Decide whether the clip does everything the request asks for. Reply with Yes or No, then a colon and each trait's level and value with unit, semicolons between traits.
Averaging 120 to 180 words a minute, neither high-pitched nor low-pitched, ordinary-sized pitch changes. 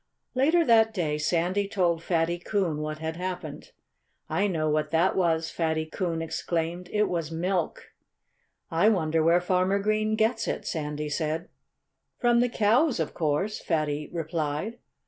Yes: average, 145 wpm; medium, 170 Hz; average, 4.3 semitones